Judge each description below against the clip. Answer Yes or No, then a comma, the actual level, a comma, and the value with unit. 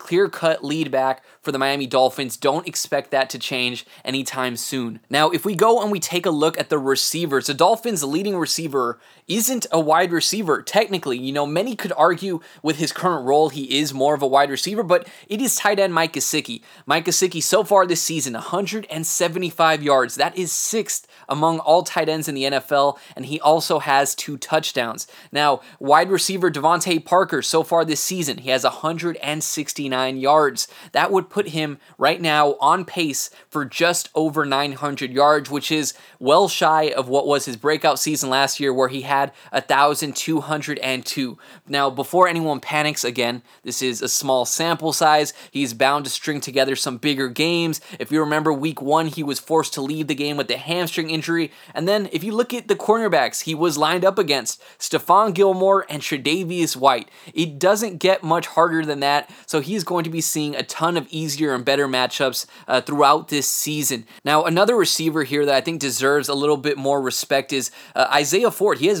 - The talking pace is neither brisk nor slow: Yes, average, 190 wpm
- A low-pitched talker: No, medium, 155 Hz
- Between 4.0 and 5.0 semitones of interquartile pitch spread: No, average, 3.5 semitones